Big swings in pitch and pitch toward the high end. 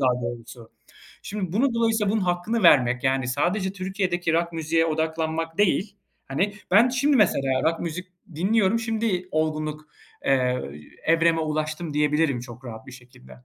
No: wide, 6.0 semitones; medium, 165 Hz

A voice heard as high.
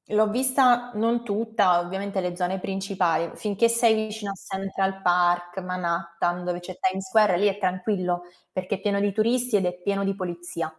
Yes: high, 195 Hz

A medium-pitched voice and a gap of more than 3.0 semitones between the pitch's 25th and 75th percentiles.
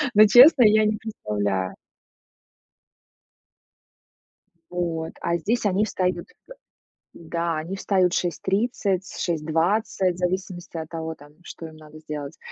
Yes: medium, 175 Hz; average, 3.7 semitones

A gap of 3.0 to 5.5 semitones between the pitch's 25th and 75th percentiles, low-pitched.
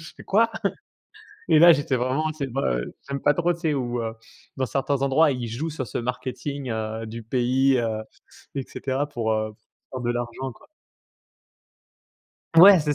Yes: average, 3.6 semitones; low, 130 Hz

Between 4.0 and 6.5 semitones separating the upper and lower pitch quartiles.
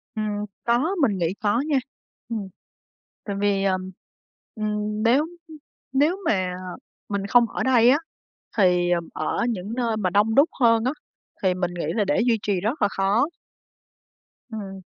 No: average, 3.5 semitones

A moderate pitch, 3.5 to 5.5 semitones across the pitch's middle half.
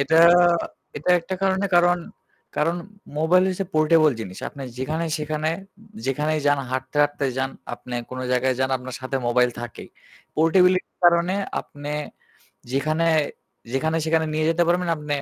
Yes: medium, 155 Hz; average, 3.8 semitones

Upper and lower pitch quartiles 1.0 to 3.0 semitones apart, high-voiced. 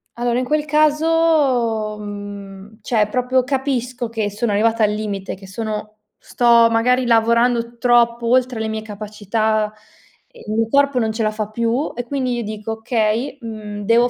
Yes: narrow, 2.6 semitones; high, 230 Hz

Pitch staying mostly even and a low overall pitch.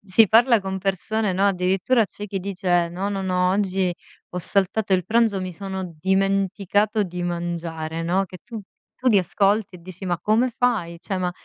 No: narrow, 2.3 semitones; high, 190 Hz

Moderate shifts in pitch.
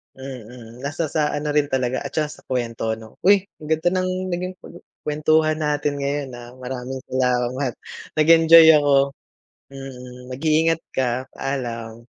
Yes: average, 3.6 semitones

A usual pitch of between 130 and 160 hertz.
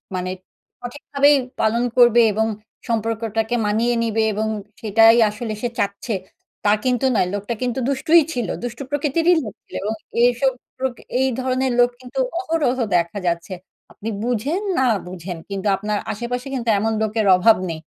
No: high, 230 Hz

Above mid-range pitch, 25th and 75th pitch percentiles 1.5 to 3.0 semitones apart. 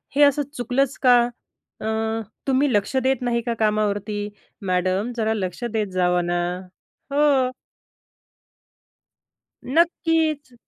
No: high, 240 Hz; average, 4.9 semitones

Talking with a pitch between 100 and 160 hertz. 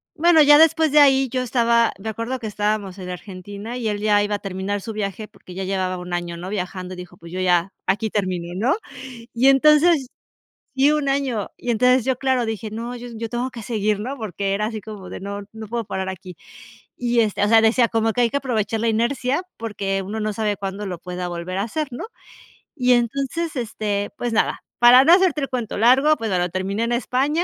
No: high, 220 Hz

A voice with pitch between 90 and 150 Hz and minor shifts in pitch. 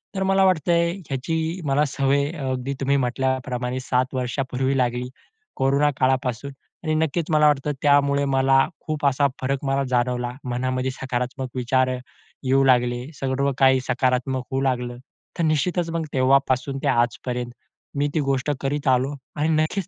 Yes: low, 135 Hz; narrow, 2.1 semitones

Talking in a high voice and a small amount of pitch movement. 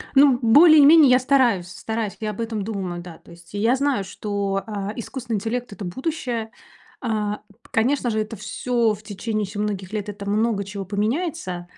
No: high, 215 Hz; average, 3.5 semitones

